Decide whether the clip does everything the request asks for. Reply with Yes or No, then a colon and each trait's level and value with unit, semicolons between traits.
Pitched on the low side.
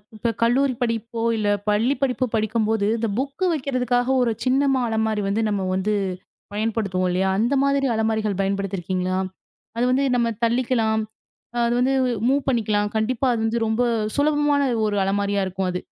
No: high, 225 Hz